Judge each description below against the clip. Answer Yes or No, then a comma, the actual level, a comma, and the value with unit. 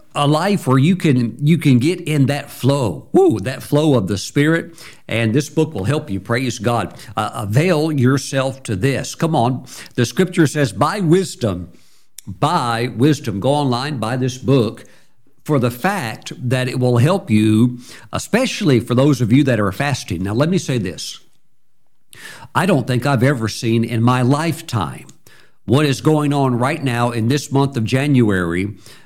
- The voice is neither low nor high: No, low, 130 Hz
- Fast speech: No, average, 175 wpm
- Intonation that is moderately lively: Yes, average, 4.0 semitones